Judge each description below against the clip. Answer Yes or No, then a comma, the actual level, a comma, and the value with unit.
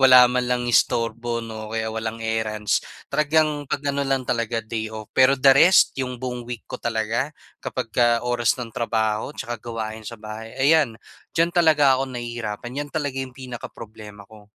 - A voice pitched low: Yes, low, 120 Hz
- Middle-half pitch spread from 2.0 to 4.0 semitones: Yes, average, 3.1 semitones